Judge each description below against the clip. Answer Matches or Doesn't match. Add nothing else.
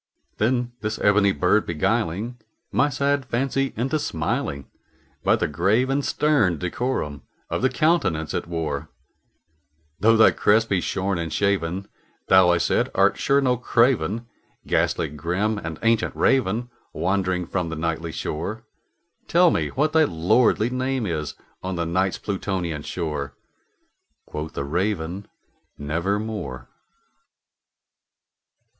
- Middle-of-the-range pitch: Doesn't match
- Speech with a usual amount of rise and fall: Doesn't match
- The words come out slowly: Matches